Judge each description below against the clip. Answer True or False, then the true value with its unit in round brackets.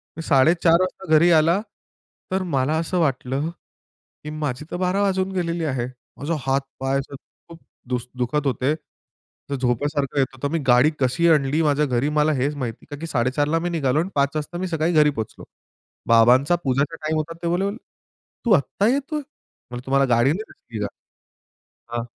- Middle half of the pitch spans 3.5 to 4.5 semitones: True (4.0 semitones)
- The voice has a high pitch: False (150 Hz)